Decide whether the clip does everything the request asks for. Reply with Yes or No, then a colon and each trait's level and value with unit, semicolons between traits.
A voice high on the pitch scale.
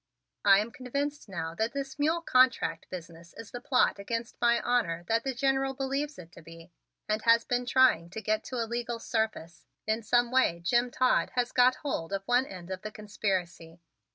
Yes: high, 230 Hz